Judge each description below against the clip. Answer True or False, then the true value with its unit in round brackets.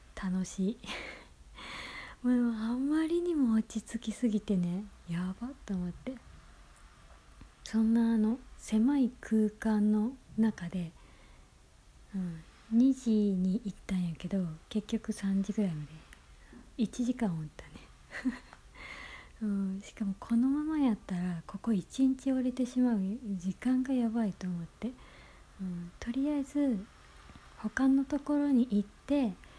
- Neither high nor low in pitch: False (220 Hz)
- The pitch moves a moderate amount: True (4.7 semitones)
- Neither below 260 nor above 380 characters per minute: False (225 characters per minute)